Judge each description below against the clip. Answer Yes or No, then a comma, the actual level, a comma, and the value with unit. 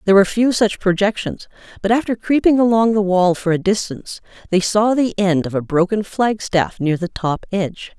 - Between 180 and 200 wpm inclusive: Yes, average, 195 wpm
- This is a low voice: No, high, 200 Hz